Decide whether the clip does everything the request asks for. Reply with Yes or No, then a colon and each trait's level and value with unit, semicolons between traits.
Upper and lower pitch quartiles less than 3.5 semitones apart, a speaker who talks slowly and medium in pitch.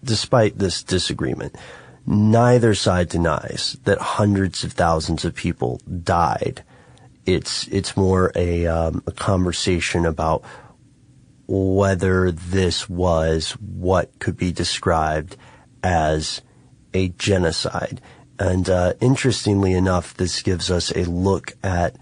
No: average, 2.9 semitones; slow, 110 wpm; very low, 95 Hz